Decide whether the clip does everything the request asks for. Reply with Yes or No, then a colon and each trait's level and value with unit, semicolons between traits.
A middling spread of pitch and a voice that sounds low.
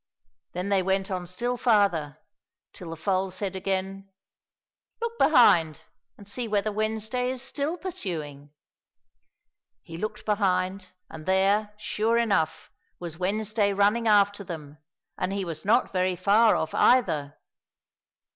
No: average, 3.4 semitones; high, 195 Hz